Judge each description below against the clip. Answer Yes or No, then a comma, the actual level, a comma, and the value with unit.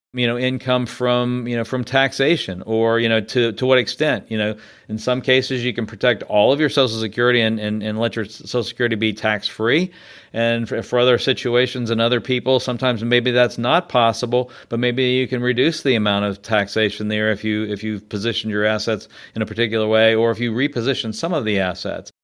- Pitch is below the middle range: Yes, low, 115 Hz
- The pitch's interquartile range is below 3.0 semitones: Yes, narrow, 2.5 semitones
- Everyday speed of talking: No, fast, 215 wpm